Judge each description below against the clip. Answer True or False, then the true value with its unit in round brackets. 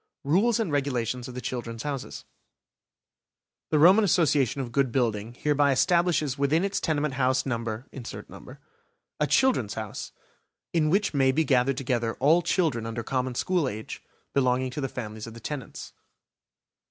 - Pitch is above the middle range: False (135 Hz)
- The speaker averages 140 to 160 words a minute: True (150 wpm)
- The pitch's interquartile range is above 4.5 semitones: False (4.0 semitones)